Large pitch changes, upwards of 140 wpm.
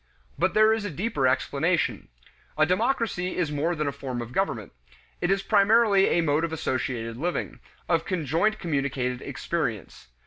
Yes: wide, 5.9 semitones; average, 160 wpm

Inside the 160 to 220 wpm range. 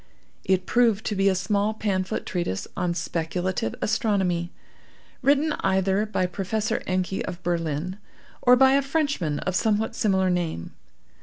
No: average, 140 wpm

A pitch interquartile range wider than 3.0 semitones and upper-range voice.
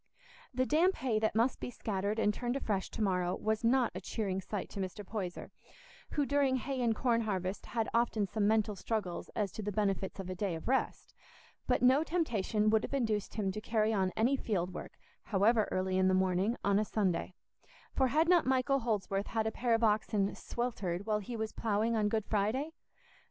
Yes: average, 3.5 semitones; high, 215 Hz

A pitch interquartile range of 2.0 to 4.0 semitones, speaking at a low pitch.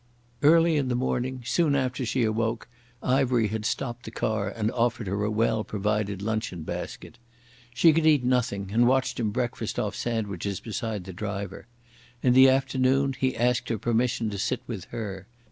Yes: average, 3.4 semitones; low, 115 Hz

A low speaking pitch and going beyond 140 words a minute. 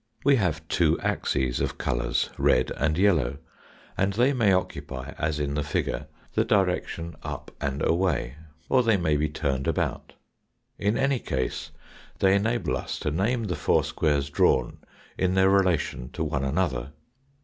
Yes: very low, 80 Hz; average, 160 wpm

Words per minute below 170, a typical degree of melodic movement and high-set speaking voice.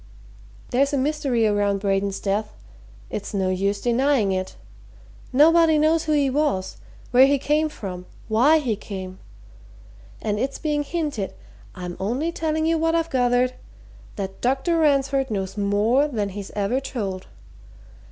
No: average, 140 wpm; wide, 6.7 semitones; high, 245 Hz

